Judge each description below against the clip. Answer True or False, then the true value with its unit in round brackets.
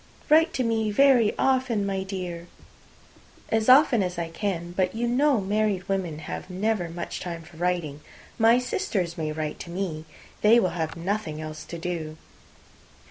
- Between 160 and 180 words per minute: True (165 wpm)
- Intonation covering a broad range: False (4.8 semitones)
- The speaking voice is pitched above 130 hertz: True (190 Hz)